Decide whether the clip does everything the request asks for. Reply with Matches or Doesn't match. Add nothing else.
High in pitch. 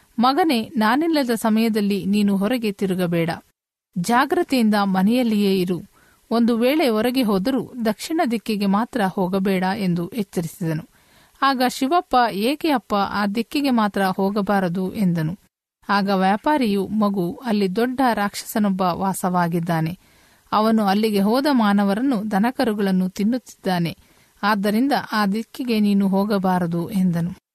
Matches